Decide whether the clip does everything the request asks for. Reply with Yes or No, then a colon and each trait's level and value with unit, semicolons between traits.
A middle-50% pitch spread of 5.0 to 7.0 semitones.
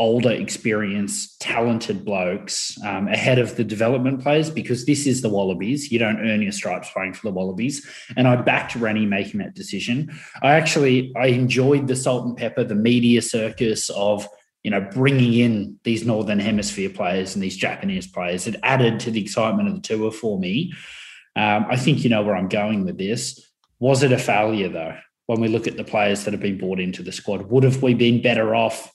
No: average, 3.7 semitones